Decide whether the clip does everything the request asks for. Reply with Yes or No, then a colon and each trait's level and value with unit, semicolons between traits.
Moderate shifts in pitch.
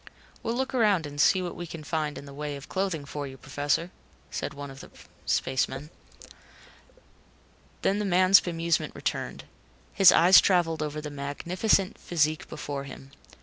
Yes: average, 4.3 semitones